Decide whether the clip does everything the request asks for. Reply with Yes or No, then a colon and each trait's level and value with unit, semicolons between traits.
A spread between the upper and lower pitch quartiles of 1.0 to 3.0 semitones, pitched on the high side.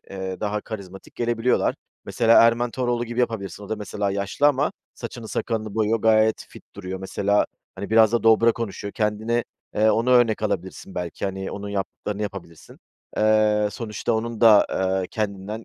No: narrow, 2.5 semitones; low, 110 Hz